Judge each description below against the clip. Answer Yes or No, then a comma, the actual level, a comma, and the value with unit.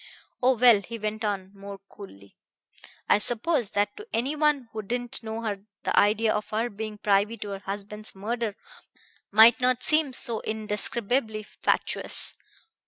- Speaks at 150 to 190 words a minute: Yes, average, 155 wpm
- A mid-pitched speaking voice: No, high, 220 Hz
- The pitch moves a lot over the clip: No, average, 2.9 semitones